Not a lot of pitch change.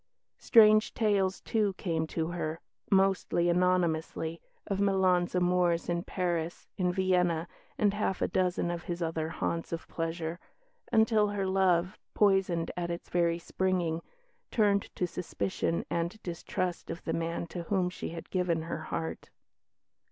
Yes: narrow, 2.2 semitones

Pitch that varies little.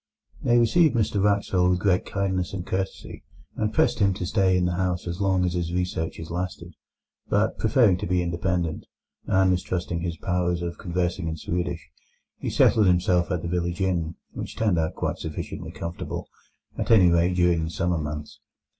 Yes: narrow, 1.7 semitones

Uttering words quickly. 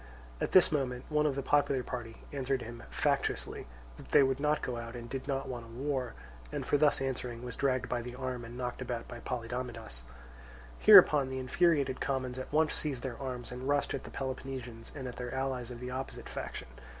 Yes: fast, 210 wpm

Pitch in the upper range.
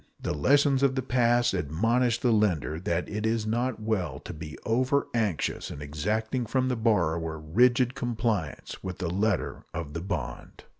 No: low, 110 Hz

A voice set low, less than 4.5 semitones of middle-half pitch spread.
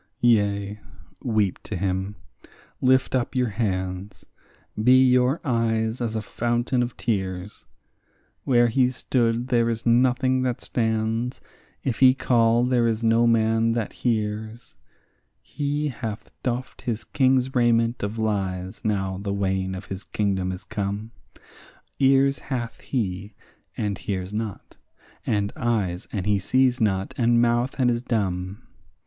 Yes: low, 115 Hz; average, 3.4 semitones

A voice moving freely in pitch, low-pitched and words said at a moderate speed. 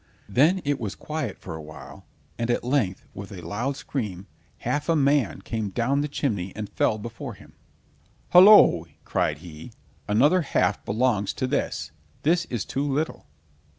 Yes: wide, 6.3 semitones; low, 120 Hz; average, 160 wpm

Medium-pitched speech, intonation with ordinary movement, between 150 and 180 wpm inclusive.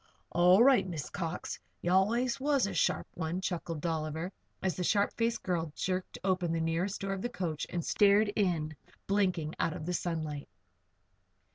Yes: medium, 180 Hz; average, 3.4 semitones; average, 170 wpm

